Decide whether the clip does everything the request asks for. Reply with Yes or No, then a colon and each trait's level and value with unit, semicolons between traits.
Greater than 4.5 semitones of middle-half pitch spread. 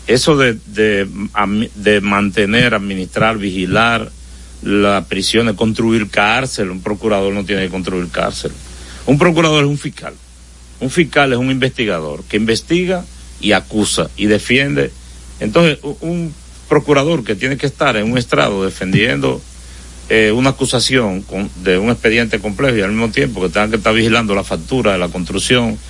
Yes: average, 5.2 semitones